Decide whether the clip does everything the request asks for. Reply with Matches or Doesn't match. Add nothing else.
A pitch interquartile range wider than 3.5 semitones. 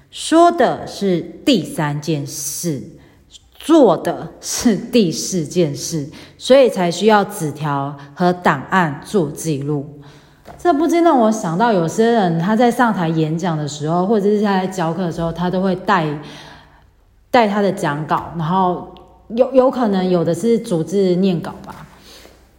Matches